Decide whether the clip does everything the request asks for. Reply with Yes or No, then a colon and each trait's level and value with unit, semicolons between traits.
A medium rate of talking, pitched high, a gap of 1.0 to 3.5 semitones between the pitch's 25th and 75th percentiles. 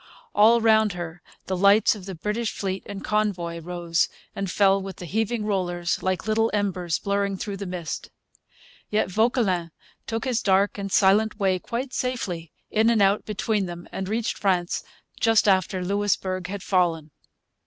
Yes: average, 165 wpm; high, 195 Hz; average, 2.9 semitones